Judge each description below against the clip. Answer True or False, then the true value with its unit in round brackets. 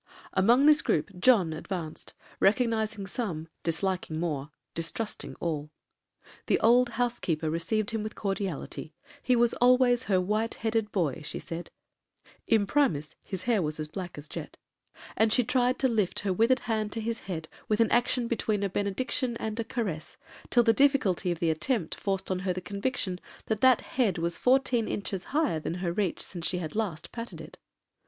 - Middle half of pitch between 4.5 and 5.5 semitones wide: True (5.2 semitones)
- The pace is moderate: True (165 wpm)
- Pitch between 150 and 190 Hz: False (205 Hz)